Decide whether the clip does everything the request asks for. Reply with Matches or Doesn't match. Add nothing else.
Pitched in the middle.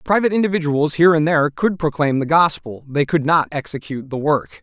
Matches